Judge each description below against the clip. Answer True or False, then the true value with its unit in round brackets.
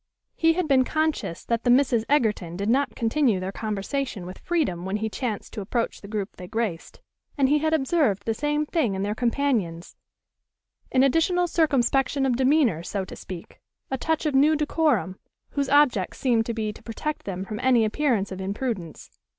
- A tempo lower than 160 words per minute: False (185 wpm)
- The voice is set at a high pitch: True (240 Hz)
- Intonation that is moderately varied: False (6.2 semitones)